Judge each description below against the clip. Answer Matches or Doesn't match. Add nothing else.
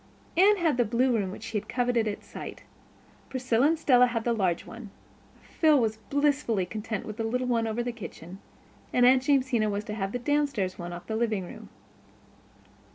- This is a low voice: Doesn't match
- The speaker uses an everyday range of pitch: Matches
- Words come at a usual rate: Matches